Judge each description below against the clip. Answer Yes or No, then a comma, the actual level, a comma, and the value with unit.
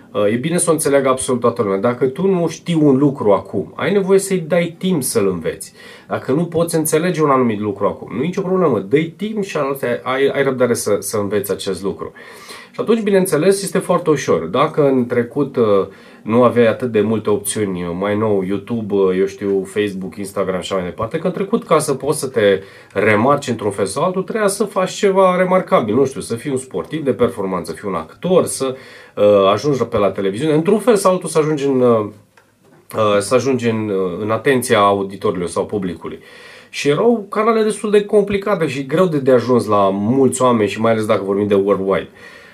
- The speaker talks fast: Yes, fast, 200 wpm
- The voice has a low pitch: Yes, low, 130 Hz